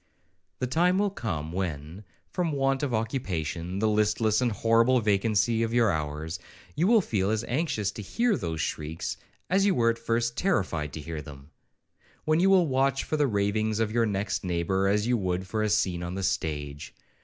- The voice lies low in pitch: Yes, low, 110 Hz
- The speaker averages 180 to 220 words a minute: Yes, average, 190 wpm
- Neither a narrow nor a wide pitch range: No, wide, 6.0 semitones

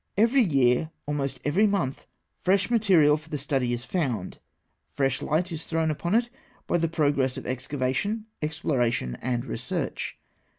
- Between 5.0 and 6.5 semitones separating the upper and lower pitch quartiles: Yes, wide, 5.5 semitones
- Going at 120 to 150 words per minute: Yes, average, 145 wpm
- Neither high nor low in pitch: Yes, medium, 150 Hz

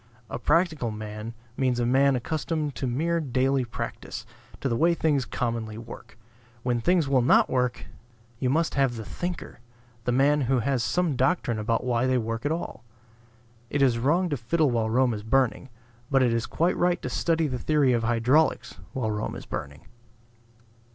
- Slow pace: No, average, 180 wpm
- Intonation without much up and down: No, average, 4.2 semitones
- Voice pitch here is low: Yes, low, 130 Hz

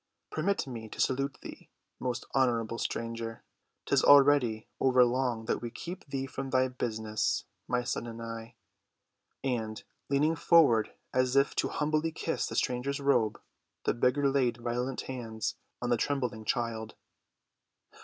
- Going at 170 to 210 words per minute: No, average, 140 wpm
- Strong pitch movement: No, average, 3.1 semitones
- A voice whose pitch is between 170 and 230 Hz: No, low, 125 Hz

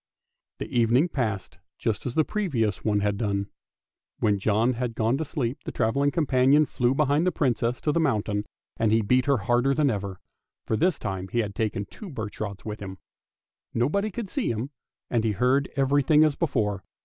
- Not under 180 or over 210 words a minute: Yes, average, 190 wpm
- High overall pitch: No, low, 120 Hz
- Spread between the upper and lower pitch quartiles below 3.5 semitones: No, average, 5.1 semitones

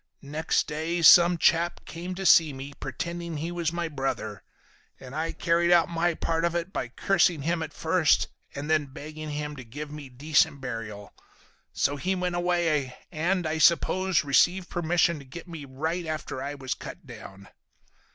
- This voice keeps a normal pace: Yes, average, 175 wpm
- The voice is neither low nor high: Yes, medium, 160 Hz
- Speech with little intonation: No, average, 3.4 semitones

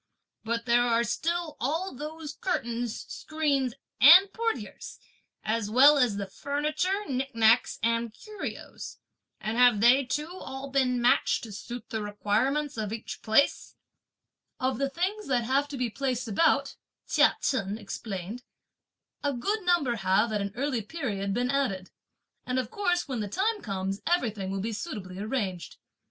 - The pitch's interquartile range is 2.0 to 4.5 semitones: No, average, 5.2 semitones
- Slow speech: No, average, 150 wpm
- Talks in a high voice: Yes, very high, 250 Hz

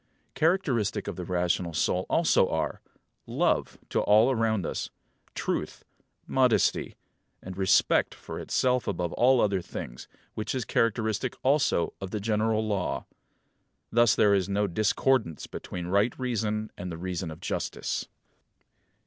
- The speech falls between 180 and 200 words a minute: No, slow, 135 wpm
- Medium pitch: No, low, 105 Hz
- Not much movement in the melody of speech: No, average, 4.0 semitones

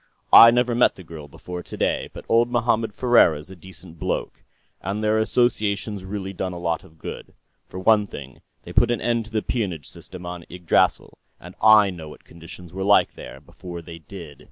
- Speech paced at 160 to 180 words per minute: No, average, 195 wpm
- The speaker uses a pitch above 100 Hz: No, very low, 95 Hz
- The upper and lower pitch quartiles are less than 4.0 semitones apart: No, average, 4.3 semitones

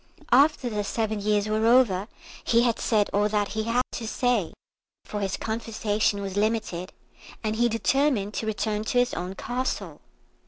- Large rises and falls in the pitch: No, narrow, 2.4 semitones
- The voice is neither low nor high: No, high, 215 Hz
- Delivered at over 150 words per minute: Yes, average, 165 wpm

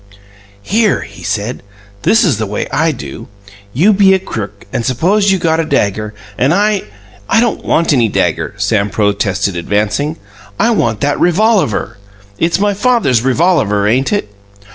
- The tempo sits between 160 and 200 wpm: Yes, average, 165 wpm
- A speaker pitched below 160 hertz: Yes, low, 135 Hz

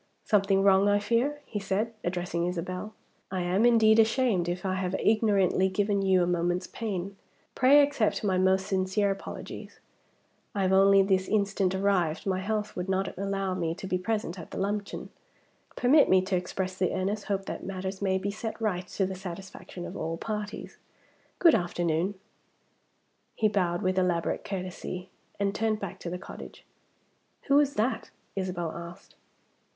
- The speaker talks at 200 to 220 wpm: No, average, 165 wpm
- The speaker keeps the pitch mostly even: Yes, narrow, 2.2 semitones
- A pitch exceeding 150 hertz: Yes, high, 190 Hz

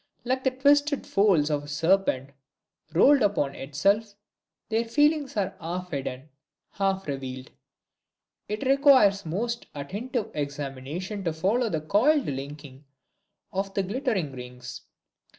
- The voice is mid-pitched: No, high, 195 Hz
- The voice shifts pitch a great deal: Yes, wide, 8.2 semitones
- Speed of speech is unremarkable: No, slow, 125 wpm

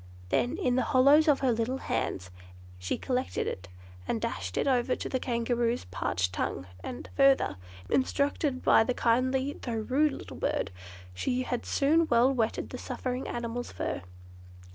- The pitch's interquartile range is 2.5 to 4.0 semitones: Yes, average, 2.8 semitones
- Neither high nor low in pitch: No, very high, 250 Hz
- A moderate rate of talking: Yes, average, 155 wpm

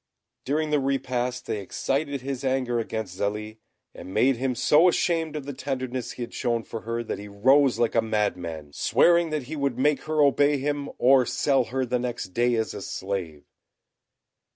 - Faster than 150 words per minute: Yes, average, 185 wpm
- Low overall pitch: Yes, low, 125 Hz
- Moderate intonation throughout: Yes, average, 4.0 semitones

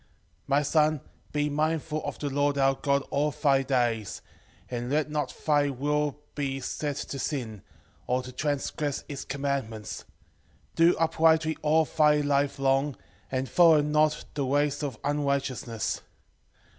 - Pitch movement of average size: No, narrow, 1.8 semitones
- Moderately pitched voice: Yes, medium, 145 Hz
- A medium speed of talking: Yes, average, 145 wpm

